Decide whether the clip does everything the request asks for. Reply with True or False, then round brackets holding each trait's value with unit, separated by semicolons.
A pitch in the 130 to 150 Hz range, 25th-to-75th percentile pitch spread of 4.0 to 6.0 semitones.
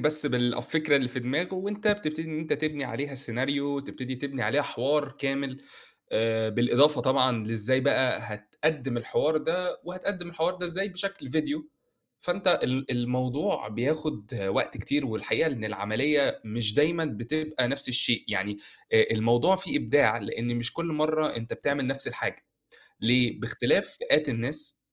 True (140 Hz; 4.4 semitones)